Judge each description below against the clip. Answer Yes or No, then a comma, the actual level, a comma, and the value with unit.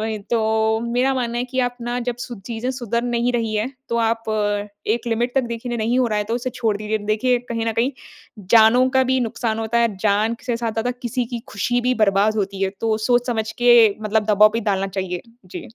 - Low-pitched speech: No, high, 230 Hz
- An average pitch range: No, narrow, 2.0 semitones